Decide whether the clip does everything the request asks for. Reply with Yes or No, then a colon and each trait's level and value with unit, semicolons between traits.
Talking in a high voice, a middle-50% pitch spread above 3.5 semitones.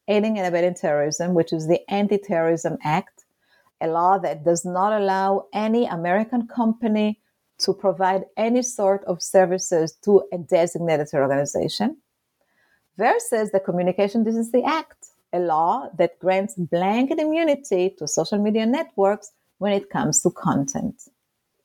Yes: high, 195 Hz; average, 3.9 semitones